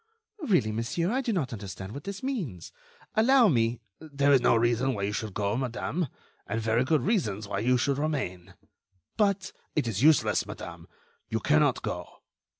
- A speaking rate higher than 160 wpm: Yes, average, 170 wpm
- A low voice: Yes, low, 130 Hz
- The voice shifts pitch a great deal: Yes, wide, 7.8 semitones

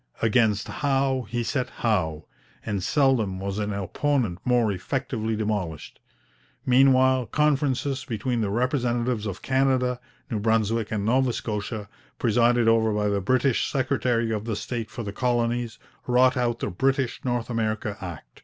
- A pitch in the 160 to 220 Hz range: No, low, 115 Hz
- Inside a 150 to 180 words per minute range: No, average, 140 wpm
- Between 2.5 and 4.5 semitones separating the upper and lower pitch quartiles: Yes, average, 3.4 semitones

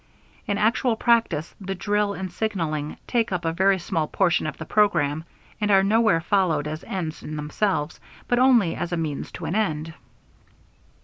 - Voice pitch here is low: No, medium, 185 Hz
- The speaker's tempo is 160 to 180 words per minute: Yes, average, 175 wpm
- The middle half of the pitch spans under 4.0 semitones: No, average, 4.8 semitones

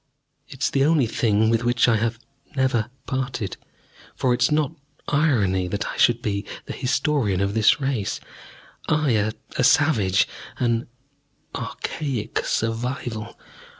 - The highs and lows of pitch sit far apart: No, average, 3.9 semitones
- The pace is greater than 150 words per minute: No, slow, 135 wpm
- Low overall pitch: Yes, low, 120 Hz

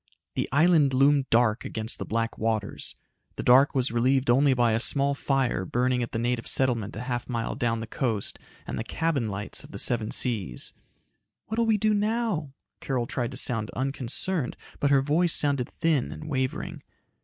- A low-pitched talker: Yes, low, 130 Hz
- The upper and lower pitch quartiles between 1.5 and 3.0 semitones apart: No, average, 3.6 semitones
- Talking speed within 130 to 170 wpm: No, average, 185 wpm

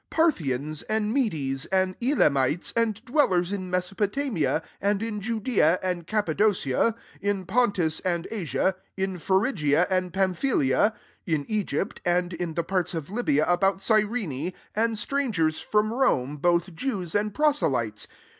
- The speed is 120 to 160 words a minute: Yes, average, 145 wpm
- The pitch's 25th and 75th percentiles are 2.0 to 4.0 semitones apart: No, average, 4.8 semitones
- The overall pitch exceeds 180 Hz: Yes, high, 190 Hz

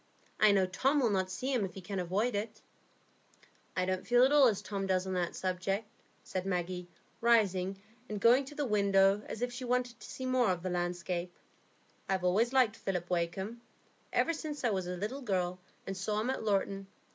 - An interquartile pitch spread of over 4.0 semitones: Yes, average, 4.5 semitones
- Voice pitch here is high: Yes, high, 195 Hz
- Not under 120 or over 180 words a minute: No, fast, 205 wpm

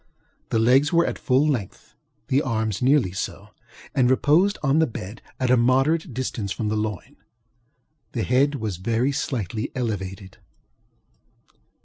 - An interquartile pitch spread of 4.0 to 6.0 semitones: Yes, average, 4.4 semitones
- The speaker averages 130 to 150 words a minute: Yes, average, 145 wpm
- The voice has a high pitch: No, low, 125 Hz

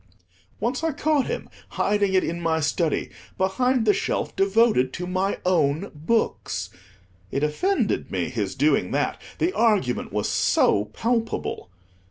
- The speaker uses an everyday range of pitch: No, wide, 6.9 semitones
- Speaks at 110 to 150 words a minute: Yes, average, 140 wpm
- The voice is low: No, high, 190 Hz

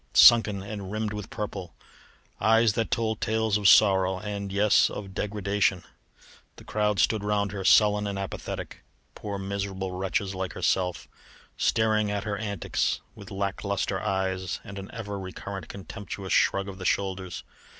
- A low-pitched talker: Yes, low, 100 Hz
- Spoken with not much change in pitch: Yes, narrow, 1.6 semitones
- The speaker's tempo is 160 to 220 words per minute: No, average, 150 wpm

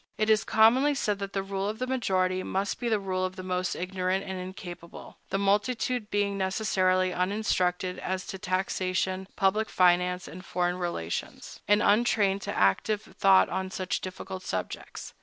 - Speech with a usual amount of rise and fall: No, narrow, 2.0 semitones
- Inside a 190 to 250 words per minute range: No, average, 165 wpm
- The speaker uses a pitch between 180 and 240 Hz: Yes, high, 190 Hz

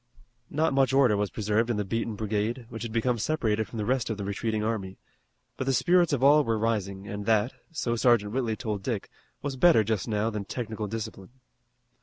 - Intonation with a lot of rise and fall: No, average, 3.3 semitones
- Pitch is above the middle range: No, low, 115 Hz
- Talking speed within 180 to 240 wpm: Yes, fast, 205 wpm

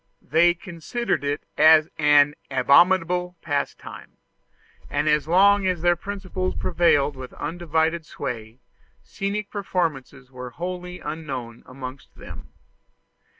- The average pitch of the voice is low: No, medium, 160 Hz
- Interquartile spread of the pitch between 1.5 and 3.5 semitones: No, average, 4.2 semitones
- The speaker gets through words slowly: Yes, slow, 105 wpm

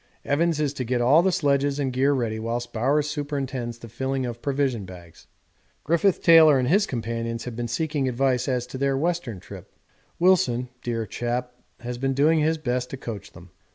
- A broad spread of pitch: No, average, 3.4 semitones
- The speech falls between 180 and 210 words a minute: Yes, average, 190 wpm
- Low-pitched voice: Yes, low, 130 Hz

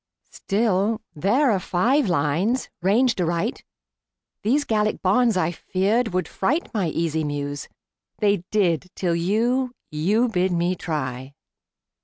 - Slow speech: Yes, slow, 125 wpm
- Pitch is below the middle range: No, high, 190 Hz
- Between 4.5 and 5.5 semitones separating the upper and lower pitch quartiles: Yes, average, 5.1 semitones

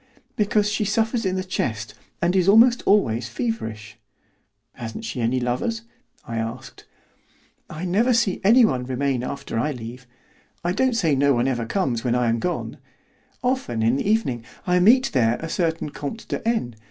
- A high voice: No, medium, 155 Hz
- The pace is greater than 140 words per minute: Yes, average, 170 wpm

